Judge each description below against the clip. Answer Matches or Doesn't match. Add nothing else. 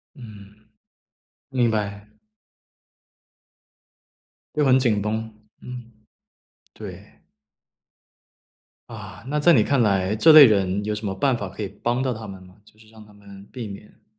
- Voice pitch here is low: Matches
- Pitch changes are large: Doesn't match